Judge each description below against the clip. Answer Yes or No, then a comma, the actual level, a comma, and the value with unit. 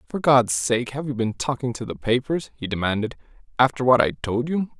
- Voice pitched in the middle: No, low, 125 Hz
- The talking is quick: Yes, fast, 215 wpm